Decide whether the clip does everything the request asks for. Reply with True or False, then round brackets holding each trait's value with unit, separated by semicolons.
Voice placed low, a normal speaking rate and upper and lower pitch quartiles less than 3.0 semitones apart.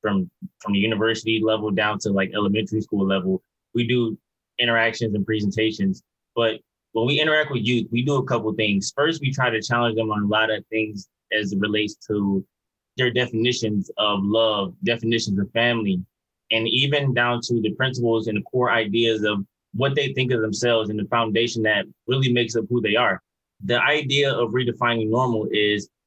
True (115 Hz; 190 wpm; 2.4 semitones)